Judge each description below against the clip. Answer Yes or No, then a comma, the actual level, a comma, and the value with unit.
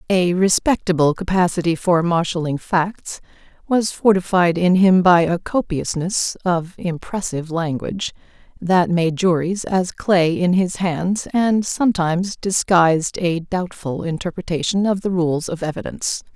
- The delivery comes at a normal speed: No, slow, 130 wpm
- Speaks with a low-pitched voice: No, medium, 180 Hz